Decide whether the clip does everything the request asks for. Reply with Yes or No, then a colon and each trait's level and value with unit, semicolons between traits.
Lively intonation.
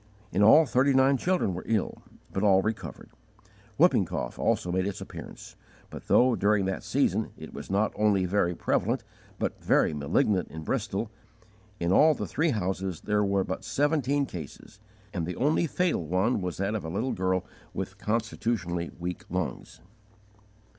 No: average, 4.8 semitones